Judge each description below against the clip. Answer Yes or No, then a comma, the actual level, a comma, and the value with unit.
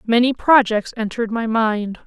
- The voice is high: Yes, high, 230 Hz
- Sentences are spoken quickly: No, average, 145 wpm